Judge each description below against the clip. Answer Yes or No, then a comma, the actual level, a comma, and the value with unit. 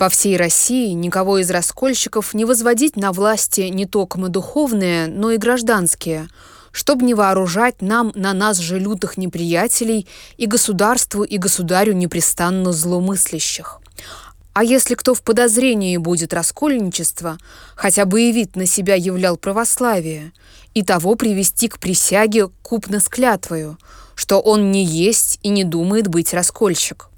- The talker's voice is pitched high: Yes, high, 195 Hz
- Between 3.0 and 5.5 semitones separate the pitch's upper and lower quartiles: Yes, average, 4.1 semitones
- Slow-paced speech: No, average, 135 wpm